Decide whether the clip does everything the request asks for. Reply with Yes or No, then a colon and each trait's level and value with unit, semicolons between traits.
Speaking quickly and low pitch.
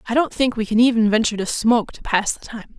No: fast, 280 wpm; high, 225 Hz